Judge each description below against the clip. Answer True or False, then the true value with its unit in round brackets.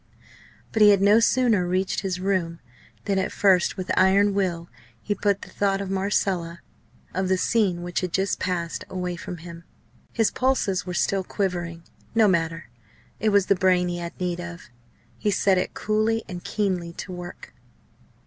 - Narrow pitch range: True (2.3 semitones)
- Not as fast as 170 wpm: False (175 wpm)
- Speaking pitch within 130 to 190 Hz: True (185 Hz)